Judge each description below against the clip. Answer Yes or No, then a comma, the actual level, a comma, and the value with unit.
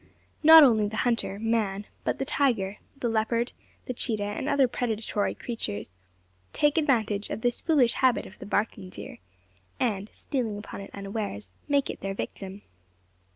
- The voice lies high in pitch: Yes, high, 220 Hz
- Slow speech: No, average, 155 wpm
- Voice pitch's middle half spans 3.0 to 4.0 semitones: Yes, average, 3.7 semitones